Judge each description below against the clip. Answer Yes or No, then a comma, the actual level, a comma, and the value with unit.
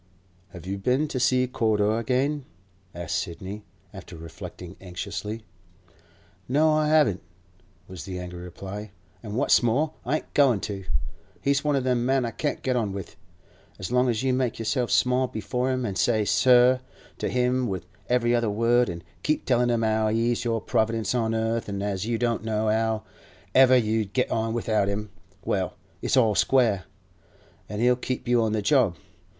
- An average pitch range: Yes, average, 3.6 semitones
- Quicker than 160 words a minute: Yes, average, 175 wpm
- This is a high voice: No, low, 115 Hz